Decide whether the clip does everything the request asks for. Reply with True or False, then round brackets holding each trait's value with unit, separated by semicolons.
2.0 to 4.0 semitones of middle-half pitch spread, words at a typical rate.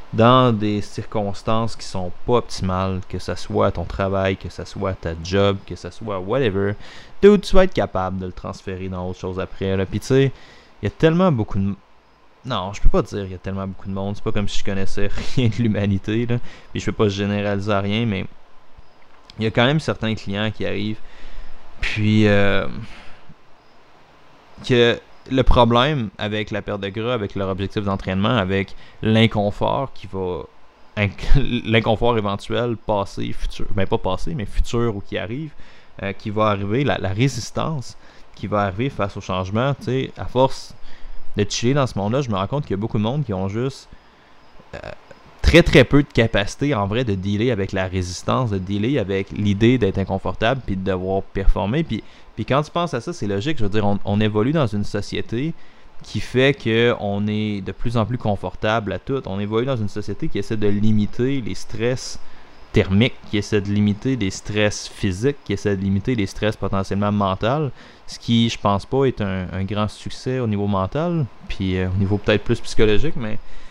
True (3.5 semitones; 200 wpm)